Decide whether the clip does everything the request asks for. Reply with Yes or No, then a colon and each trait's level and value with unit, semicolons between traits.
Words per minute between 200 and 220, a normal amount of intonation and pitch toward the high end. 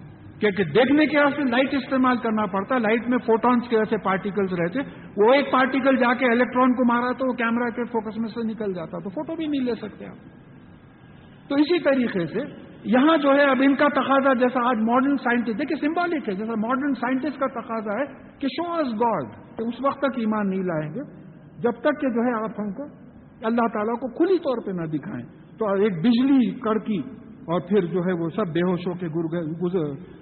Yes: fast, 205 wpm; average, 4.7 semitones; high, 235 Hz